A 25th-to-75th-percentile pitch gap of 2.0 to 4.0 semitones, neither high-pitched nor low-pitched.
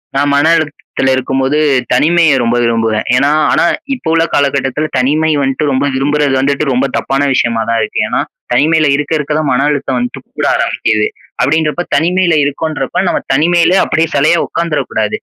Yes: average, 3.1 semitones; medium, 145 Hz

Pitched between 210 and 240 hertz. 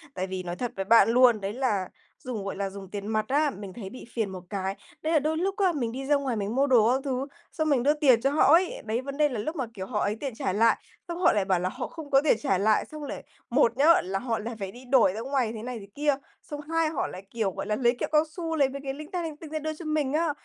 No: very high, 255 Hz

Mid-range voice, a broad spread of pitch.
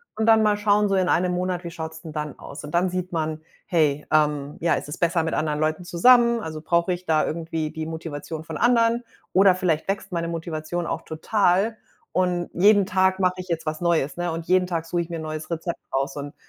No: medium, 170 Hz; average, 2.7 semitones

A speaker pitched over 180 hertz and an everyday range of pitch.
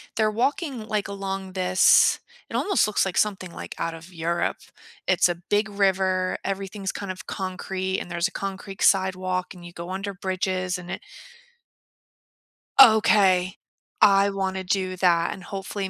No: high, 190 Hz; narrow, 1.4 semitones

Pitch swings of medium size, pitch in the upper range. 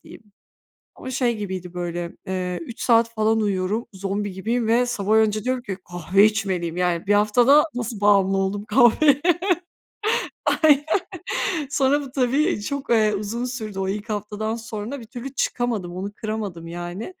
Yes: average, 3.9 semitones; high, 215 Hz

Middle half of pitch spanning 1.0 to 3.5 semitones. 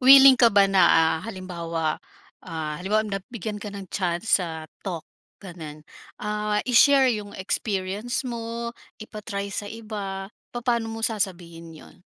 No: average, 3.9 semitones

